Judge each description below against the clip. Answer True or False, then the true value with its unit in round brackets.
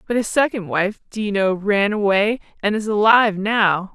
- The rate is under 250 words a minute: True (200 wpm)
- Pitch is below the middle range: False (205 Hz)